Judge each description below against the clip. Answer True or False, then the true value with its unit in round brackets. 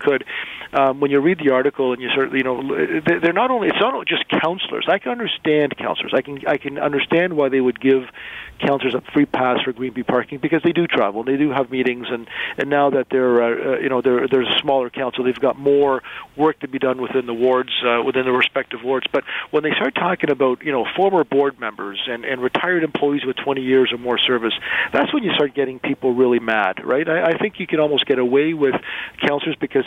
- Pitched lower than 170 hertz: True (135 Hz)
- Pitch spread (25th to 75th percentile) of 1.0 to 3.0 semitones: True (2.4 semitones)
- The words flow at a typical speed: False (235 wpm)